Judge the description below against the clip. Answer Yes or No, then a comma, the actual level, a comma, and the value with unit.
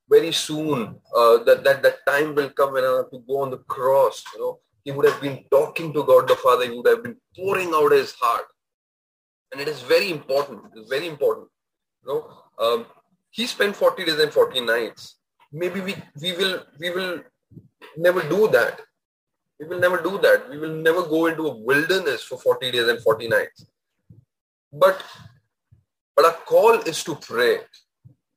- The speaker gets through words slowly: No, average, 190 wpm